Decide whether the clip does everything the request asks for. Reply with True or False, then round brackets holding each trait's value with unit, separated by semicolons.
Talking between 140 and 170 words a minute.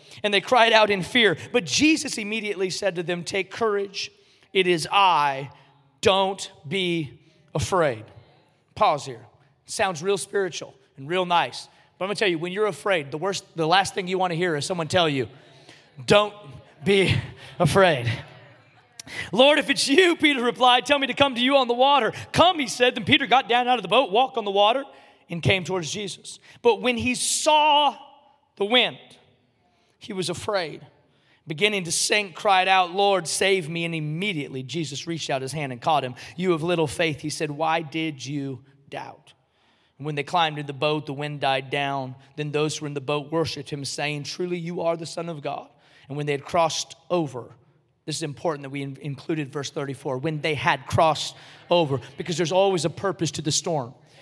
False (200 wpm)